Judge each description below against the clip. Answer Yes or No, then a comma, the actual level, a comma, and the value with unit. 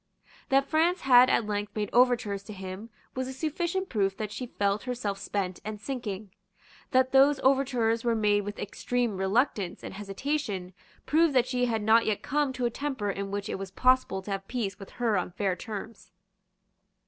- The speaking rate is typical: Yes, average, 185 wpm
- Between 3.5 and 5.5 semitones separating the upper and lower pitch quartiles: Yes, average, 4.5 semitones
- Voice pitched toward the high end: Yes, high, 225 Hz